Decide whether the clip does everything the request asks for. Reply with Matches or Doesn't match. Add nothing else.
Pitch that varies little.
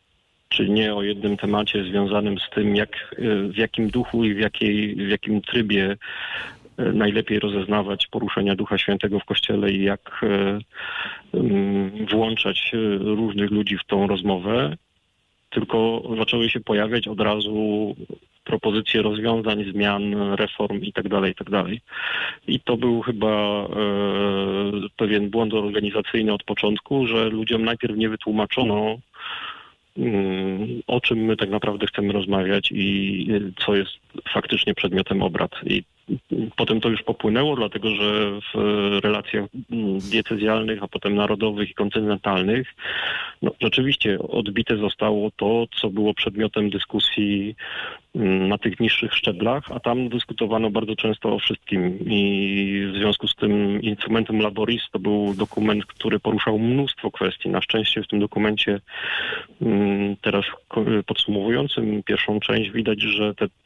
Matches